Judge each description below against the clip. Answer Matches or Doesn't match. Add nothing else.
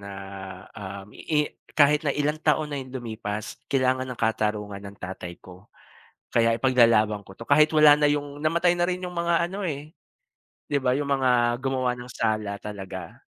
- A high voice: Doesn't match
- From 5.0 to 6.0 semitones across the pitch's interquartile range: Matches